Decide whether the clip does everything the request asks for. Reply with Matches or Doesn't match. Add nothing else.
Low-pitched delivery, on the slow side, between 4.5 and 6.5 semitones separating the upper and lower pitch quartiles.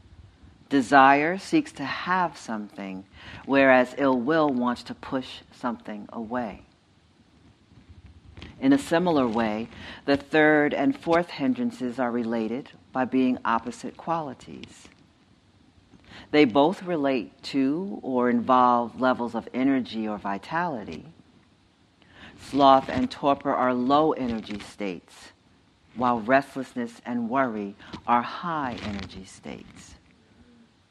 Matches